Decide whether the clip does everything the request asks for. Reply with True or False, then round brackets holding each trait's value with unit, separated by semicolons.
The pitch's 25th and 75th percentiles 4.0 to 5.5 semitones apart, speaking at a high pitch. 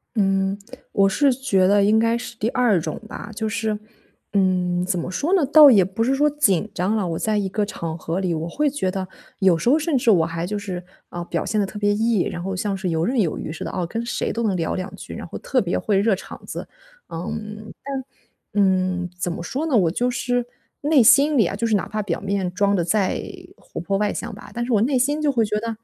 True (4.3 semitones; 205 Hz)